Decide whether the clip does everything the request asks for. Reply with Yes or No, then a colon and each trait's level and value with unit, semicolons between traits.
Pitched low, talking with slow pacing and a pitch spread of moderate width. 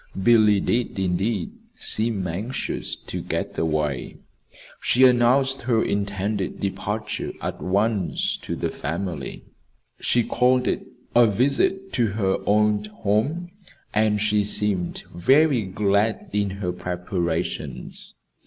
Yes: low, 105 Hz; slow, 115 wpm; average, 3.8 semitones